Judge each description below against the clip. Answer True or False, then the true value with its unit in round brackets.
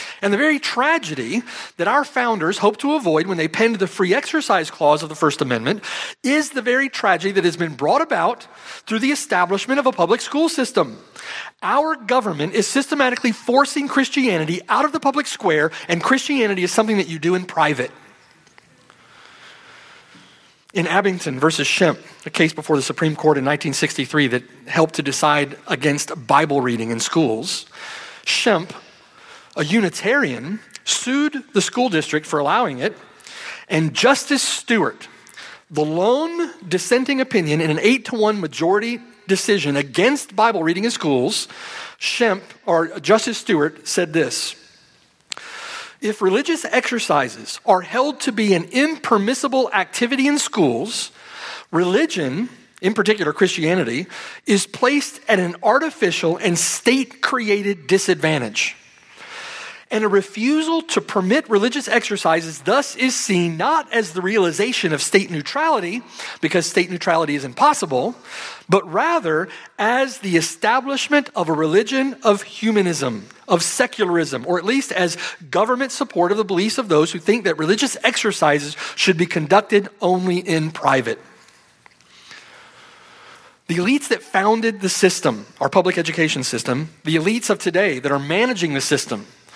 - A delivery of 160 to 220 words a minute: False (145 wpm)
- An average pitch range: False (7.5 semitones)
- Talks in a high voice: True (200 Hz)